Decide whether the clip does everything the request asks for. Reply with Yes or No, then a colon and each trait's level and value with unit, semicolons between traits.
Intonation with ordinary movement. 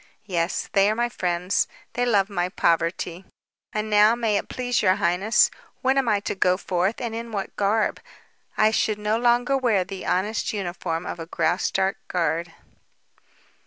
Yes: average, 3.8 semitones